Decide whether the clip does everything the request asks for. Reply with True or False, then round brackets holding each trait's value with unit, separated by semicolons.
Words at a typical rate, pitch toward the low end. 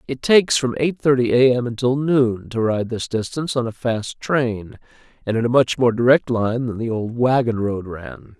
False (215 wpm; 120 Hz)